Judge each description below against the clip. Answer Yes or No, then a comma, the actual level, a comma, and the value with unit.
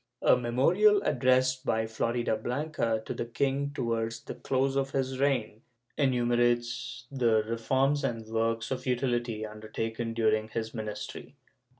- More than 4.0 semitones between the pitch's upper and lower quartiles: No, average, 2.7 semitones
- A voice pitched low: Yes, low, 120 Hz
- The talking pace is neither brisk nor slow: No, slow, 125 wpm